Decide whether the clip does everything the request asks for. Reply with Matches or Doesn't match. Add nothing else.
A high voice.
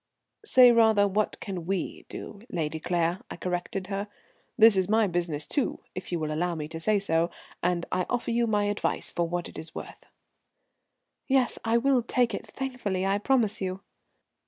Matches